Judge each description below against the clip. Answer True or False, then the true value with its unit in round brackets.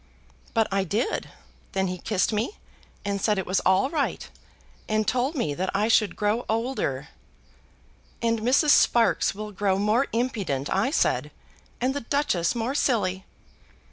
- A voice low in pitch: False (215 Hz)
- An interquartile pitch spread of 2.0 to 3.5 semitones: False (4.2 semitones)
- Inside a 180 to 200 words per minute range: False (150 wpm)